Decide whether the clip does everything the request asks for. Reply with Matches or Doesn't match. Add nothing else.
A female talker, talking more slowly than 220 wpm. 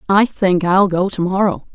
Matches